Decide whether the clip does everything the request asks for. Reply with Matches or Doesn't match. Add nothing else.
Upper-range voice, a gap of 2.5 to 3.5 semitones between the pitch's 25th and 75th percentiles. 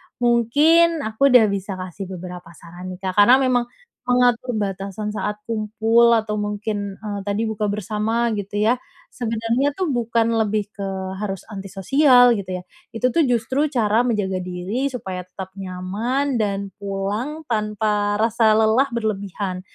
Matches